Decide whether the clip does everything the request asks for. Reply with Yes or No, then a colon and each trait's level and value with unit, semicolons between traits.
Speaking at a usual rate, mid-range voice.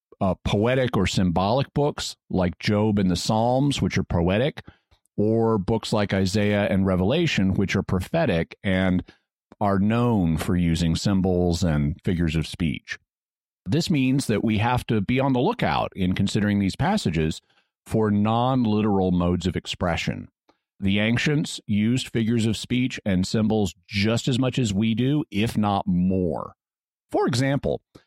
No: average, 150 wpm; low, 105 Hz